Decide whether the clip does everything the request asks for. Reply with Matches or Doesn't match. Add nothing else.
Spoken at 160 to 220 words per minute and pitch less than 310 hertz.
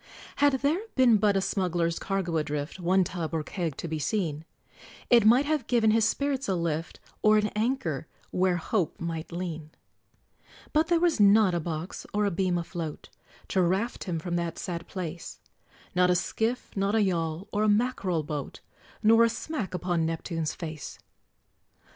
Matches